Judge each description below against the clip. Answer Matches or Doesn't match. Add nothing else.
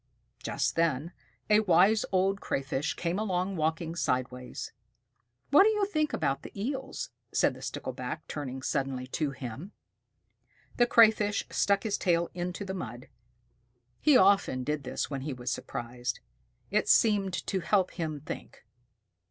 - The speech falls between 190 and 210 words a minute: Doesn't match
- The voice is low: Doesn't match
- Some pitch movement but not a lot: Doesn't match